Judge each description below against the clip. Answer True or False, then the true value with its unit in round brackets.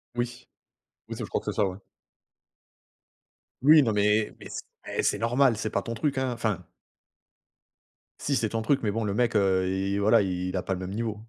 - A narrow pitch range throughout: False (3.4 semitones)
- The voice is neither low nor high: False (110 Hz)